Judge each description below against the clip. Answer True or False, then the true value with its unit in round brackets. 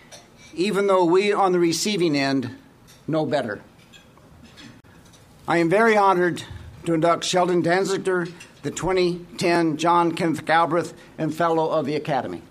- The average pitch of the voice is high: False (170 Hz)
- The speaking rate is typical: False (130 wpm)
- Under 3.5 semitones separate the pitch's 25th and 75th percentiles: True (2.7 semitones)